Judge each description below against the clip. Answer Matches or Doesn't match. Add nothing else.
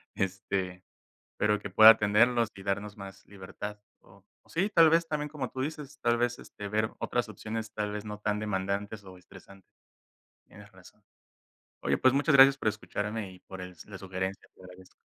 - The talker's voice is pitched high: Doesn't match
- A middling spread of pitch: Matches